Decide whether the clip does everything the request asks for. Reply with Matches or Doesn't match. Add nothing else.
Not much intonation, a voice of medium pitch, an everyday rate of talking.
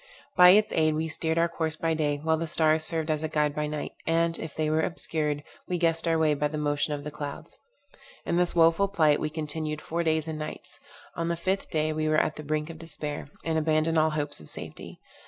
Doesn't match